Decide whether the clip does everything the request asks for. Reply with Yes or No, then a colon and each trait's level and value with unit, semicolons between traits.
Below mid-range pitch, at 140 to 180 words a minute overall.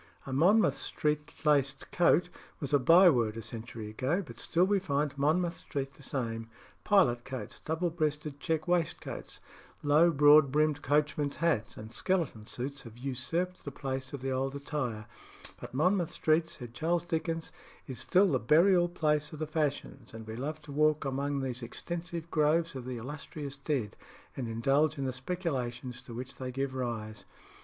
No: medium, 145 Hz; average, 170 wpm